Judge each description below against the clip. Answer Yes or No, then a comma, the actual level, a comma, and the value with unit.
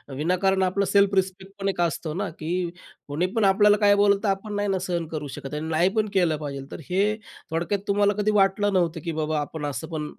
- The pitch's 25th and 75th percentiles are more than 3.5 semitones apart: Yes, average, 4.0 semitones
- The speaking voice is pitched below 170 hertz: No, medium, 185 Hz